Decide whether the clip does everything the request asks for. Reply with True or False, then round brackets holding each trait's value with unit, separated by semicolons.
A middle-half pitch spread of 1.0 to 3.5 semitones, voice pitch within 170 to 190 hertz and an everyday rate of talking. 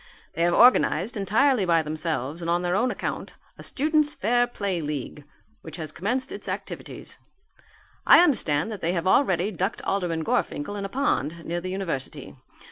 False (5.6 semitones; 185 Hz; 170 wpm)